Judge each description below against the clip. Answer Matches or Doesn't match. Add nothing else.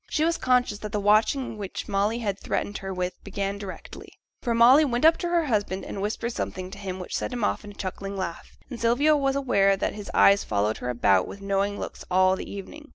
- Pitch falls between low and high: Doesn't match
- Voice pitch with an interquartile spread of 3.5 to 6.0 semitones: Matches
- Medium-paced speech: Doesn't match